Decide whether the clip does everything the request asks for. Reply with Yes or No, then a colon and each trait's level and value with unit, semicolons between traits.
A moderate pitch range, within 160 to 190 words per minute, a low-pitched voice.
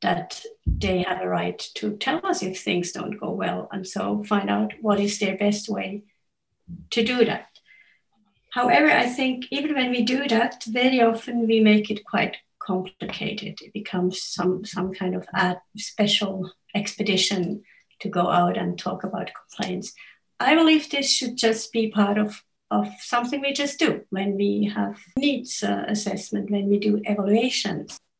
No: average, 3.8 semitones; average, 170 wpm; high, 210 Hz